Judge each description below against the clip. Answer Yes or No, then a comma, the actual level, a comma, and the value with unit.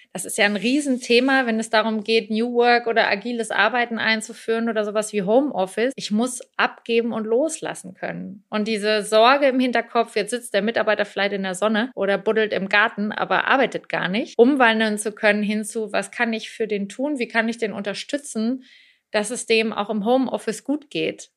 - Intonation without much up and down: Yes, narrow, 2.2 semitones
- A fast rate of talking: Yes, fast, 195 wpm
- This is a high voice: Yes, high, 225 Hz